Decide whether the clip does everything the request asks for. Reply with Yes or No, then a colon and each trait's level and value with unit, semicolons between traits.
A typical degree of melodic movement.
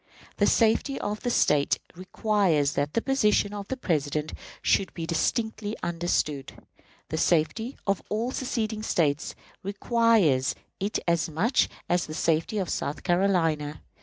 No: wide, 5.7 semitones